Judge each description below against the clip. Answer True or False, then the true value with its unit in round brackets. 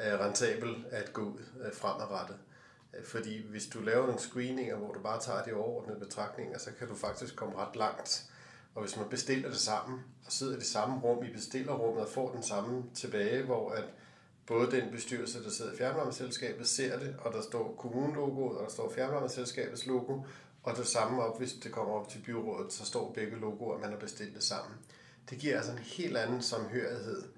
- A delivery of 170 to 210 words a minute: True (200 wpm)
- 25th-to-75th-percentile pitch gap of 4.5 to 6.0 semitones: False (2.6 semitones)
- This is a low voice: True (120 Hz)